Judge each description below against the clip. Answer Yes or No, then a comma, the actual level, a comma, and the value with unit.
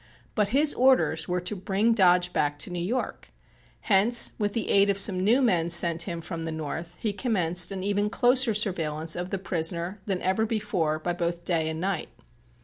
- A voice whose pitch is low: No, medium, 185 Hz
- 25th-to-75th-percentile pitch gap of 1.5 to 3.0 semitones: No, average, 3.7 semitones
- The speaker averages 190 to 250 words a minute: Yes, average, 195 wpm